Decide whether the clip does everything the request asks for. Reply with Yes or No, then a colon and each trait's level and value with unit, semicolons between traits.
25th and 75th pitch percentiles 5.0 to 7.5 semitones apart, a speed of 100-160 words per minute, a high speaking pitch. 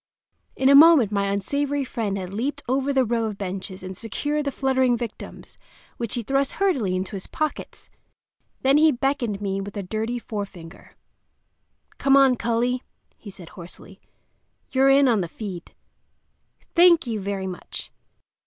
Yes: wide, 5.6 semitones; average, 155 wpm; high, 235 Hz